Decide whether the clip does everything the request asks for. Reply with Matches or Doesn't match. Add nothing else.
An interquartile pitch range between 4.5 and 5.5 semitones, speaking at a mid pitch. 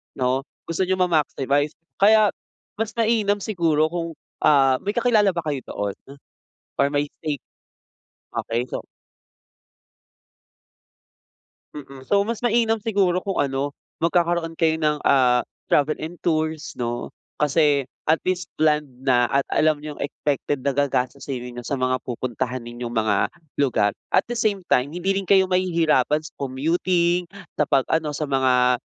Matches